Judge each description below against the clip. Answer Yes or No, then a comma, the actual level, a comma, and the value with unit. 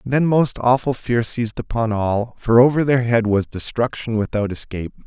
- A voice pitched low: Yes, low, 115 Hz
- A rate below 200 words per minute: Yes, average, 180 wpm